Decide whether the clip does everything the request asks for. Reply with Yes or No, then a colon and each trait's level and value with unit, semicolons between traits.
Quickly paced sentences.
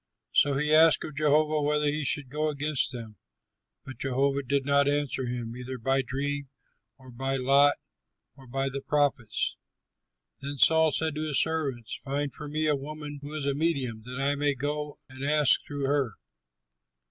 No: average, 175 wpm